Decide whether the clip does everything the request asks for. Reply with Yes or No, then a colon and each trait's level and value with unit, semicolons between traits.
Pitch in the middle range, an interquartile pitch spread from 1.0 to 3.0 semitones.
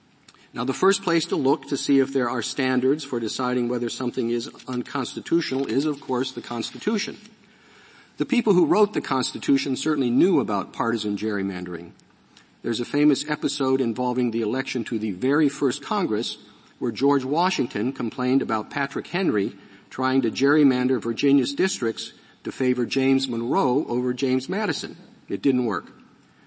No: low, 130 Hz; average, 2.7 semitones